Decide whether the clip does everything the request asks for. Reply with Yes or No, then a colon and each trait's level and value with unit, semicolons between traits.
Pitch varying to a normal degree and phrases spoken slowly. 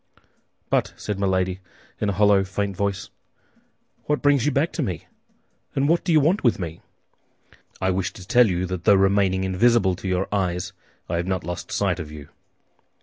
No: average, 3.2 semitones; average, 185 wpm